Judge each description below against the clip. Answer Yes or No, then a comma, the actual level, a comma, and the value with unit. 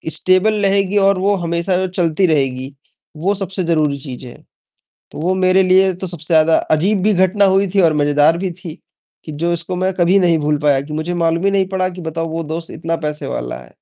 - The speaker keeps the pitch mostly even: No, average, 3.3 semitones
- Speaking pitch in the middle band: Yes, medium, 170 Hz